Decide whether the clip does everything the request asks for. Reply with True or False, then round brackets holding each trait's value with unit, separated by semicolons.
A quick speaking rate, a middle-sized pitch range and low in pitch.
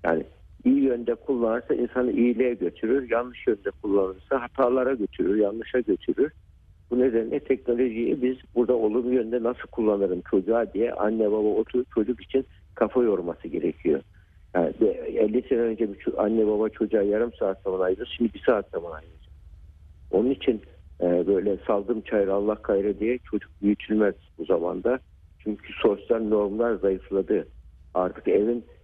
True (145 wpm; 4.5 semitones; 110 Hz)